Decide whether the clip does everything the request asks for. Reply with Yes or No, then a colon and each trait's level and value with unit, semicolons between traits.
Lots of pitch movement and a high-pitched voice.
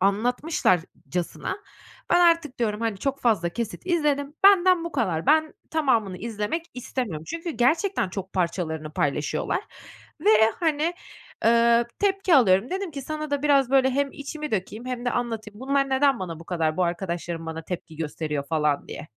Yes: wide, 8.3 semitones; high, 235 Hz